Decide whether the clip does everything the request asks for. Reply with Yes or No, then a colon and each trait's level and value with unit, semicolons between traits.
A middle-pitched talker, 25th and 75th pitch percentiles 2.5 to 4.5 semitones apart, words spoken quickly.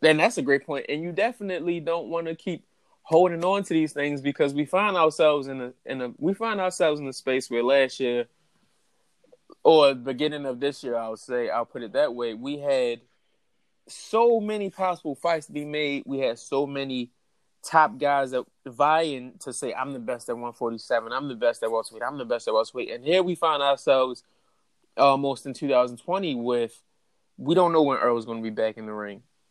No: medium, 145 Hz; average, 5.3 semitones; fast, 210 wpm